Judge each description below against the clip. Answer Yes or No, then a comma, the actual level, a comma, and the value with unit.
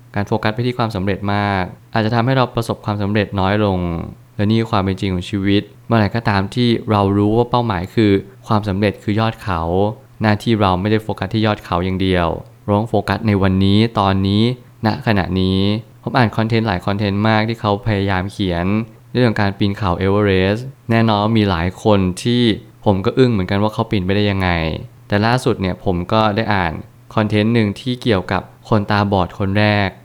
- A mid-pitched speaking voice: No, low, 105 Hz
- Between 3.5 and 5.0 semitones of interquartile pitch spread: No, narrow, 2.5 semitones